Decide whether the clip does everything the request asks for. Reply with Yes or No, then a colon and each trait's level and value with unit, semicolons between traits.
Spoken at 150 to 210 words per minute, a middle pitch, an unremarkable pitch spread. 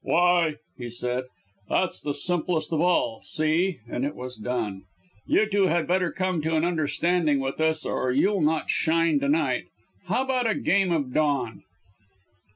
Yes: average, 165 wpm; medium, 160 Hz; average, 4.8 semitones